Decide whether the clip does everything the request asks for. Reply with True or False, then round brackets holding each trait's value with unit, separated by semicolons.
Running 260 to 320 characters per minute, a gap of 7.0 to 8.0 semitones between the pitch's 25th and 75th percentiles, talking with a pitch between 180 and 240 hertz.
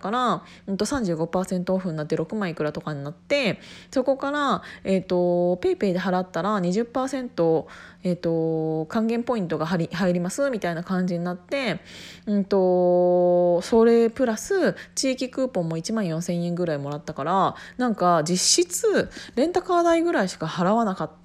False (300 characters per minute; 5.3 semitones; 185 Hz)